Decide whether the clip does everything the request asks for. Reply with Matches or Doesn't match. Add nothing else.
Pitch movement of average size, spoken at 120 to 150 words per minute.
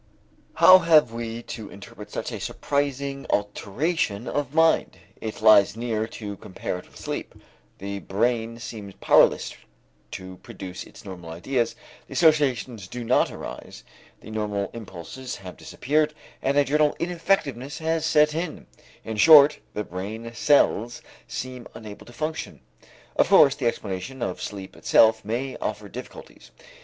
Doesn't match